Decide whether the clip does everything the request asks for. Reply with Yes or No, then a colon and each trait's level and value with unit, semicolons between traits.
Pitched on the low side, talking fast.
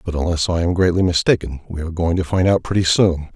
Yes: very low, 85 Hz; fast, 250 wpm